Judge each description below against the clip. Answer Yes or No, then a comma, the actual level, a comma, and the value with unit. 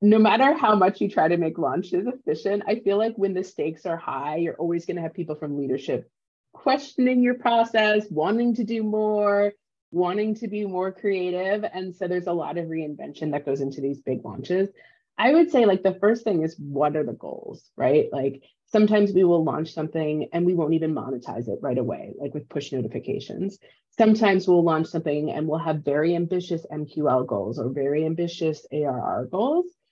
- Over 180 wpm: Yes, average, 195 wpm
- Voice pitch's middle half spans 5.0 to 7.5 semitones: Yes, wide, 5.5 semitones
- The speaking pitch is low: No, medium, 175 Hz